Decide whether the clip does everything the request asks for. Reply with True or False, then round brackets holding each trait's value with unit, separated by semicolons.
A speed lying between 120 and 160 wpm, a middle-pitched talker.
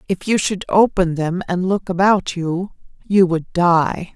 False (175 wpm; 180 Hz)